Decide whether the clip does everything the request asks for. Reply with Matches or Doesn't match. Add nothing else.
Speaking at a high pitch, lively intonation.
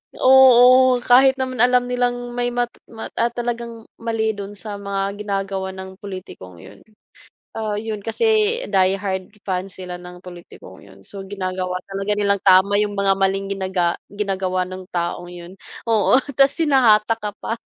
Doesn't match